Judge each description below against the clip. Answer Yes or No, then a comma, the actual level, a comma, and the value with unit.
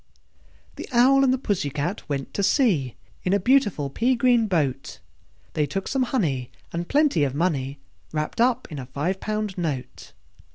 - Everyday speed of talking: Yes, average, 170 wpm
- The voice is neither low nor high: Yes, medium, 180 Hz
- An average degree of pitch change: No, wide, 9.0 semitones